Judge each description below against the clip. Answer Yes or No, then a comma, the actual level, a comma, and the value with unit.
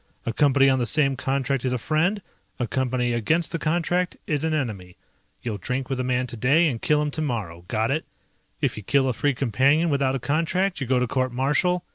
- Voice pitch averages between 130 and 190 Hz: Yes, low, 135 Hz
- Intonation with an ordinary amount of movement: Yes, average, 3.8 semitones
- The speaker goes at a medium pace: No, fast, 215 wpm